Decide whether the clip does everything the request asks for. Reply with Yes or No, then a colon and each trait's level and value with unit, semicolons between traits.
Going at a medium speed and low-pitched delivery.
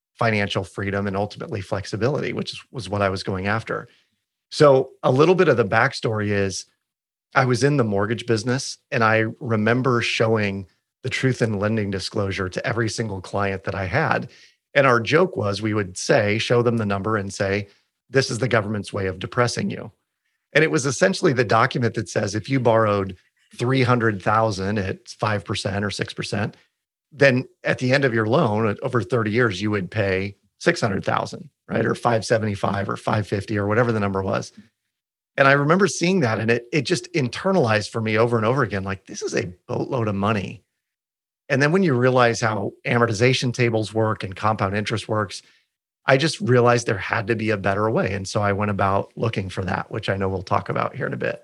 Yes: average, 195 wpm; low, 110 Hz